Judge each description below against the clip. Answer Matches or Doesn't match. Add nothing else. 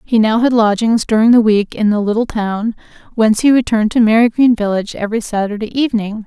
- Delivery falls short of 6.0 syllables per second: Doesn't match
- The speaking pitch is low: Doesn't match